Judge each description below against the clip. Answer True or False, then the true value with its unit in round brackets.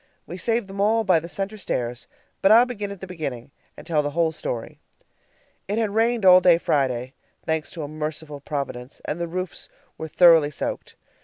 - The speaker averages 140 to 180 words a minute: False (190 wpm)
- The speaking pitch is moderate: True (170 Hz)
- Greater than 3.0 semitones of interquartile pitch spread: True (5.1 semitones)